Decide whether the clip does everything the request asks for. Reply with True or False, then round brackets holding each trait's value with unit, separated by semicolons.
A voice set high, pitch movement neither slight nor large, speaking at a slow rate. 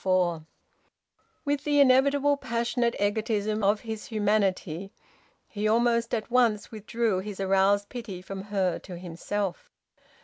True (210 Hz; 3.3 semitones; 125 wpm)